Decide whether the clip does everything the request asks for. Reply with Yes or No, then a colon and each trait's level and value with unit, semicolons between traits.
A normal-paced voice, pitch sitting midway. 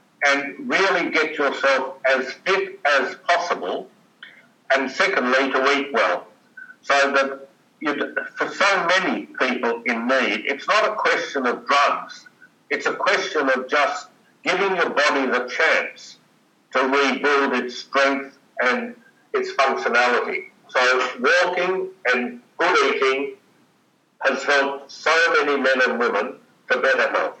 No: slow, 130 wpm; medium, 145 Hz